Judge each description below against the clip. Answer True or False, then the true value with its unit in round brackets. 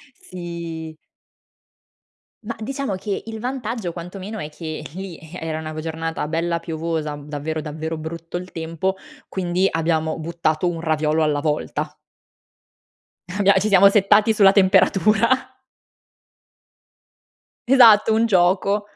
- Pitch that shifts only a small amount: False (4.0 semitones)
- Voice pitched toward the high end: False (175 Hz)